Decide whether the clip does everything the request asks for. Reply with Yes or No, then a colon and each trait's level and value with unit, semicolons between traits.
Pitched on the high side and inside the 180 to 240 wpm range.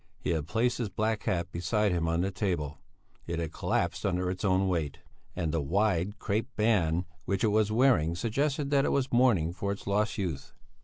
No: very low, 95 Hz; average, 200 wpm